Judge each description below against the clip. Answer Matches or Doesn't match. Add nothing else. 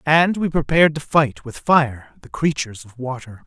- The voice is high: Doesn't match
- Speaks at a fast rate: Doesn't match